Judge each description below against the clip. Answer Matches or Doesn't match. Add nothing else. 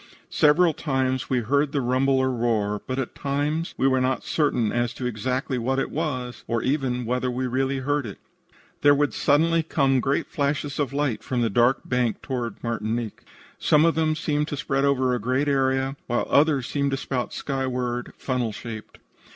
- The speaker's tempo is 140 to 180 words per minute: Doesn't match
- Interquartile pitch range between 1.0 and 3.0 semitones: Matches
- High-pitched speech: Doesn't match